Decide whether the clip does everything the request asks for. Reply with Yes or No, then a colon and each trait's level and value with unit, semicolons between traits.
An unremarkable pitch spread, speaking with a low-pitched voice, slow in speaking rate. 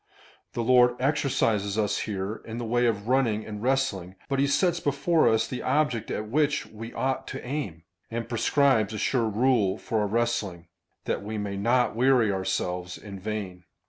No: average, 4.1 semitones; low, 115 Hz; average, 180 wpm